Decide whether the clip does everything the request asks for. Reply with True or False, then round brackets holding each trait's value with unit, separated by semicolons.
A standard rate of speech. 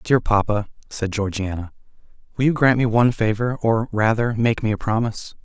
True (175 wpm)